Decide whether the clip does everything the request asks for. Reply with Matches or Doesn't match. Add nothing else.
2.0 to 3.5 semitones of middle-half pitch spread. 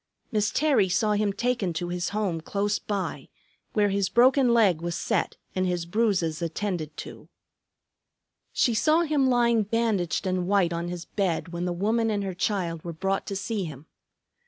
Doesn't match